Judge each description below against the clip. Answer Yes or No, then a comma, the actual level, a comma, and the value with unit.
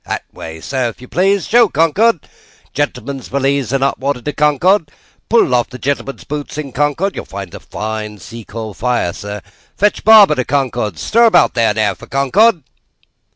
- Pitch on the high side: No, low, 135 Hz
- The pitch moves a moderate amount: No, wide, 5.9 semitones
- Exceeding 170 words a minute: Yes, average, 180 wpm